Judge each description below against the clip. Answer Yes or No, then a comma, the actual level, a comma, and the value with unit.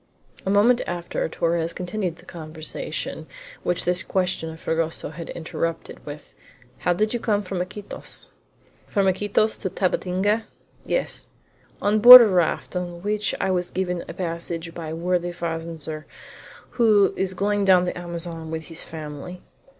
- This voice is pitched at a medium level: Yes, medium, 180 Hz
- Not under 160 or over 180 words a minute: No, average, 150 wpm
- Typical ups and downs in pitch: Yes, average, 3.2 semitones